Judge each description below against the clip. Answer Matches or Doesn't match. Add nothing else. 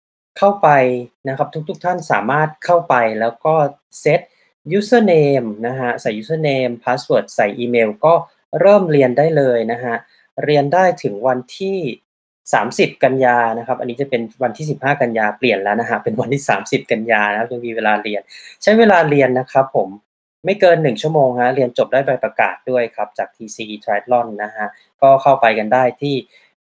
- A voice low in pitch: Matches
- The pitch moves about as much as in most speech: Matches